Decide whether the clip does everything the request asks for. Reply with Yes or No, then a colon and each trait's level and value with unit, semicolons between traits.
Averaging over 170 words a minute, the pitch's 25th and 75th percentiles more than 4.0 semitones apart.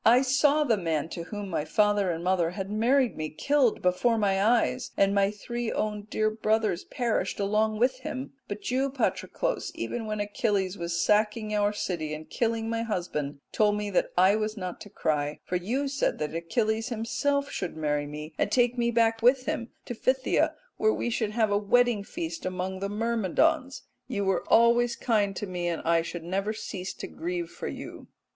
Yes: average, 195 wpm; average, 4.4 semitones